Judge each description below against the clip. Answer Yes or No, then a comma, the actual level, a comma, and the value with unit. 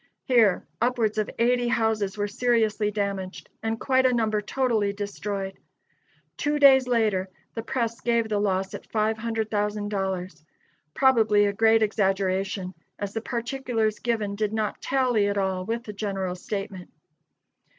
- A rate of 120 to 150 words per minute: Yes, average, 140 wpm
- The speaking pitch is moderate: No, high, 215 Hz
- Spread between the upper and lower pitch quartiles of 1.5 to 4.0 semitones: Yes, narrow, 2.6 semitones